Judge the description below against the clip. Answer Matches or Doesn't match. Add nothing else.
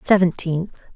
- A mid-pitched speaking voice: Matches